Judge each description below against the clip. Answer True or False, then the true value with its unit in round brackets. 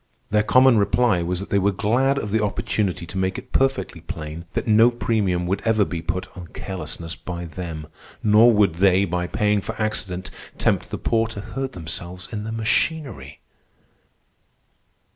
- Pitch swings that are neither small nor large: True (4.0 semitones)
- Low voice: True (100 Hz)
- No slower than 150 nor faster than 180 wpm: True (170 wpm)